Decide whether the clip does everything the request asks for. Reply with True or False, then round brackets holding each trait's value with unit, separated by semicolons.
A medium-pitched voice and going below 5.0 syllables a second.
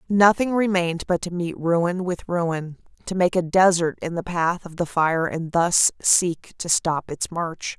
True (175 Hz; 4.0 syllables/s)